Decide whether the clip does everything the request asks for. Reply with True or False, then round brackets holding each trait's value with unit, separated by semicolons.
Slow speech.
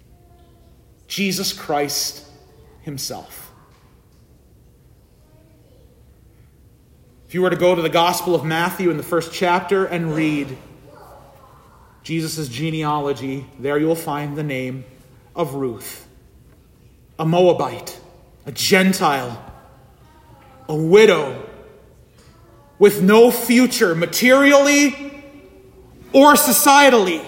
True (90 wpm)